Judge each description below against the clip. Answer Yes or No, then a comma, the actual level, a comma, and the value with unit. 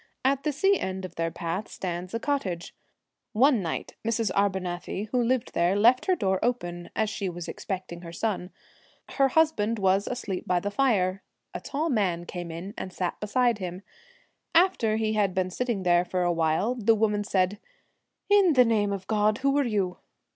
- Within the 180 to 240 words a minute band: Yes, average, 190 wpm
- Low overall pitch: No, high, 205 Hz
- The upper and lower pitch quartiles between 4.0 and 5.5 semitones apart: Yes, average, 4.7 semitones